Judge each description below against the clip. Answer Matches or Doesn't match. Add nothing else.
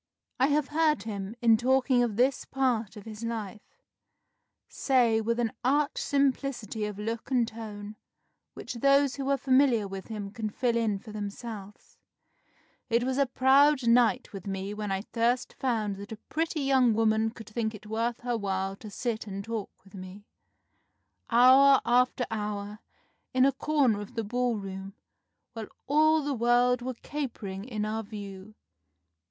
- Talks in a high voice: Matches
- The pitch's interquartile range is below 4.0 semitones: Matches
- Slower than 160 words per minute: Doesn't match